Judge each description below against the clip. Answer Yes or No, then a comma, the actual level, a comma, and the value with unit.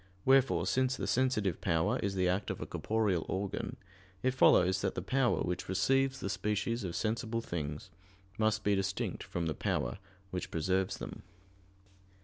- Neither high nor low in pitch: No, low, 100 Hz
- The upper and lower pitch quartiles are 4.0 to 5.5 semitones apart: Yes, average, 4.3 semitones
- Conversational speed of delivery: Yes, average, 160 wpm